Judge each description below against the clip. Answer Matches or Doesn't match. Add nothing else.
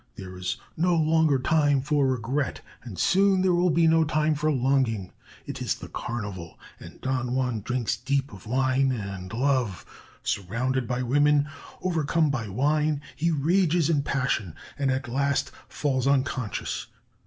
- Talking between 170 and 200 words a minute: Doesn't match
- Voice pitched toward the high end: Doesn't match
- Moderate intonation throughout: Matches